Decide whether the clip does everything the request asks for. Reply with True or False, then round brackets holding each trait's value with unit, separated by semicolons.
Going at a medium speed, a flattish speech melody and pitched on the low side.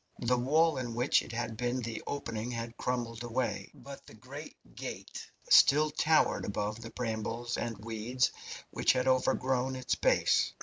True (160 wpm; 2.1 semitones; 120 Hz)